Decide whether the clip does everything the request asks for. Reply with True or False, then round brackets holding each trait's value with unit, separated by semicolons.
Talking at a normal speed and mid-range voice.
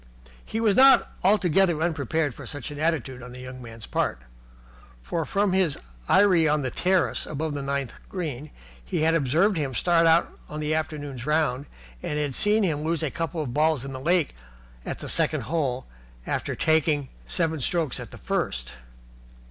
True (180 wpm; 155 Hz)